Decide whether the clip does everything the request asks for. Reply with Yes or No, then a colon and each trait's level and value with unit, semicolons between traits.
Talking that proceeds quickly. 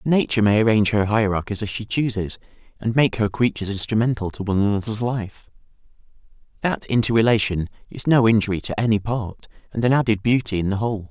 No: average, 175 wpm